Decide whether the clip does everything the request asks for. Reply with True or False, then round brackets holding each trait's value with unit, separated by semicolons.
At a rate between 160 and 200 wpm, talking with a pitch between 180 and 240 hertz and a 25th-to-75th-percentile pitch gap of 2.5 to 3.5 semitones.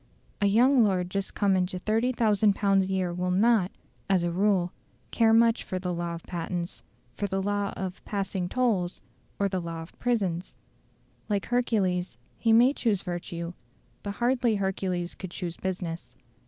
True (165 wpm; 190 Hz; 3.2 semitones)